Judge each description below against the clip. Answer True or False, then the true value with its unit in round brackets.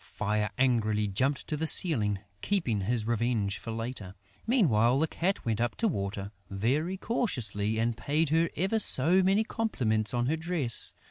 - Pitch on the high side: False (120 Hz)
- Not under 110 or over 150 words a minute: False (160 wpm)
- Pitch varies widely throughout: True (7.3 semitones)